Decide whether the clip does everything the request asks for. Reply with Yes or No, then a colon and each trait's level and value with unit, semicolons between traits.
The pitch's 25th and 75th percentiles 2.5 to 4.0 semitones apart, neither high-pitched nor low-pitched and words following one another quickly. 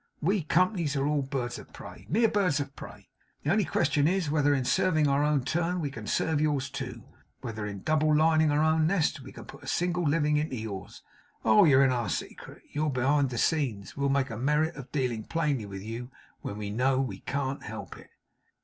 Yes: average, 3.5 semitones; medium, 145 Hz; fast, 215 wpm